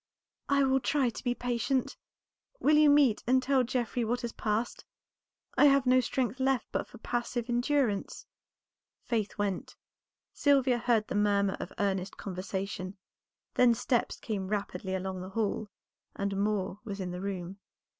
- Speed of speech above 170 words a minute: No, average, 155 wpm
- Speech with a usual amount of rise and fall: Yes, average, 4.4 semitones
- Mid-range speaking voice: No, high, 230 Hz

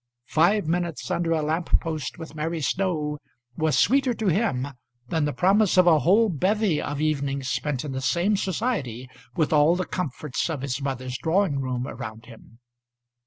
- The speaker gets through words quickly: No, average, 170 wpm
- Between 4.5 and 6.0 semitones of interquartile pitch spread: Yes, average, 4.8 semitones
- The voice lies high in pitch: No, medium, 155 Hz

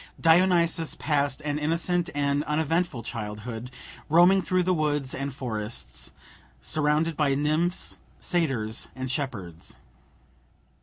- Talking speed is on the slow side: Yes, slow, 105 wpm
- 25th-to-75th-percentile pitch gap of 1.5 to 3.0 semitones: No, average, 4.7 semitones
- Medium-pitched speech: Yes, medium, 150 Hz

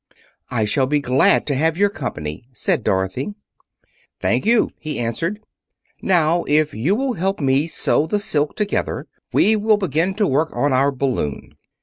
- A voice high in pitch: No, medium, 155 Hz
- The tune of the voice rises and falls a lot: Yes, wide, 6.7 semitones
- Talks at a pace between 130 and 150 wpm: No, average, 160 wpm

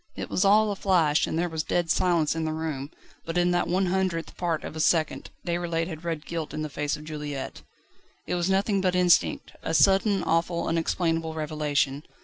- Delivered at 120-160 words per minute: No, average, 200 wpm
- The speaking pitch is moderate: Yes, medium, 165 Hz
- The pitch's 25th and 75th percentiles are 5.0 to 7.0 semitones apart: No, narrow, 2.4 semitones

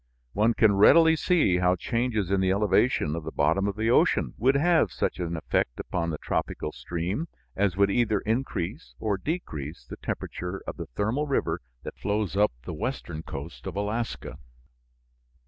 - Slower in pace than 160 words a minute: No, average, 170 wpm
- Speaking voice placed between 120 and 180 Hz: No, low, 100 Hz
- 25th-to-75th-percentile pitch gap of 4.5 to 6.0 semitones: Yes, average, 5.1 semitones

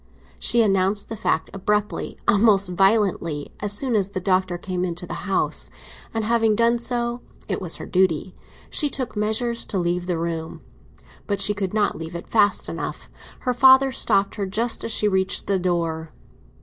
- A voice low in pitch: No, high, 200 Hz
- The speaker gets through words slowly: No, average, 170 wpm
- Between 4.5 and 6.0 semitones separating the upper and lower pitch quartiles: No, average, 3.7 semitones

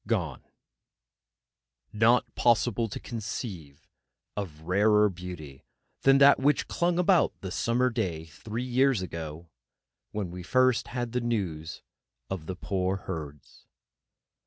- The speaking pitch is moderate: No, low, 105 Hz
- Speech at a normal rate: No, slow, 120 wpm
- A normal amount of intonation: No, wide, 6.2 semitones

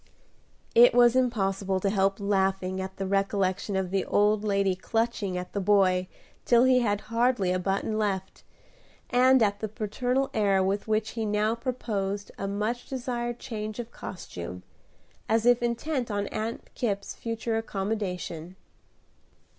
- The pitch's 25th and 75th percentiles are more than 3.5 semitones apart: No, average, 3.2 semitones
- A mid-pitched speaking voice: No, high, 210 Hz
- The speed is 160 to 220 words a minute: No, average, 145 wpm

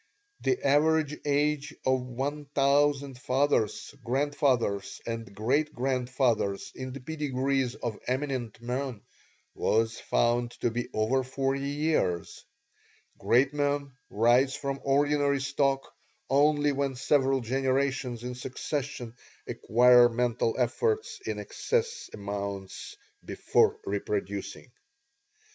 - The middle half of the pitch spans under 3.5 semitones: Yes, average, 3.0 semitones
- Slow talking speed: Yes, slow, 105 wpm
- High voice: No, low, 130 Hz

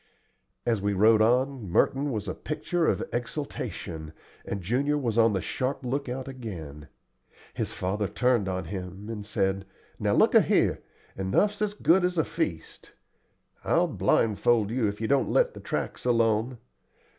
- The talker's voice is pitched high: No, low, 115 Hz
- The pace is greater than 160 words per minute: No, average, 155 wpm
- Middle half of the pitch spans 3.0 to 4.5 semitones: No, wide, 5.4 semitones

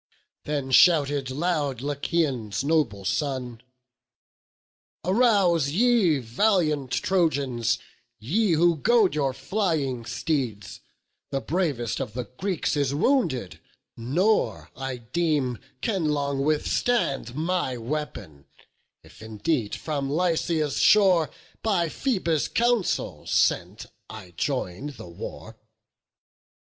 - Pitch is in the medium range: Yes, medium, 145 Hz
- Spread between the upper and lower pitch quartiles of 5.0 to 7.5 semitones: Yes, wide, 5.4 semitones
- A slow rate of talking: Yes, slow, 100 wpm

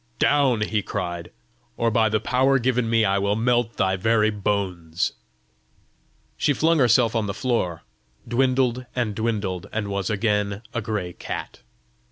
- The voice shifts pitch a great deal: No, average, 3.4 semitones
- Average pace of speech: Yes, average, 150 wpm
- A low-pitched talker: Yes, low, 110 Hz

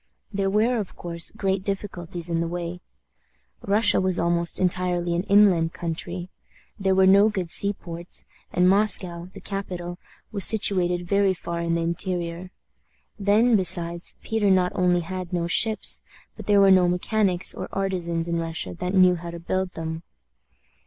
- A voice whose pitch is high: No, medium, 180 Hz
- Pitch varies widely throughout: No, narrow, 2.4 semitones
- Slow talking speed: No, average, 160 wpm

